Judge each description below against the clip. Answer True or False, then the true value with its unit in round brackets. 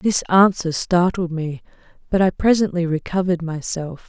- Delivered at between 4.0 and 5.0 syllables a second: True (4.8 syllables/s)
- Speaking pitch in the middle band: True (175 Hz)